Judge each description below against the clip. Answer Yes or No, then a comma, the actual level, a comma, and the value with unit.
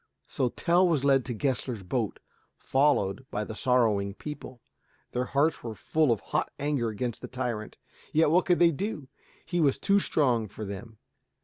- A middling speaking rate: Yes, average, 175 wpm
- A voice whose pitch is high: No, low, 130 Hz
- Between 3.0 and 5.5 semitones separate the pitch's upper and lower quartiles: Yes, average, 5.0 semitones